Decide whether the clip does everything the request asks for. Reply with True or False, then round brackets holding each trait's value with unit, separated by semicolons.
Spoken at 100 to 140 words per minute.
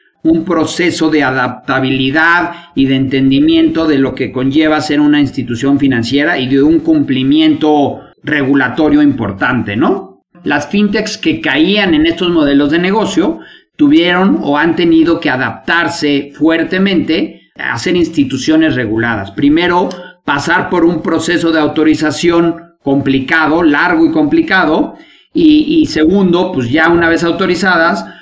True (130 wpm)